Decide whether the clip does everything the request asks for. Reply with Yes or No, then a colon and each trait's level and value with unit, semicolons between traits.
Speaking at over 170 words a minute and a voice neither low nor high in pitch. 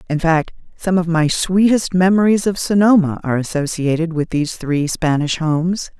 No: average, 160 wpm; medium, 170 Hz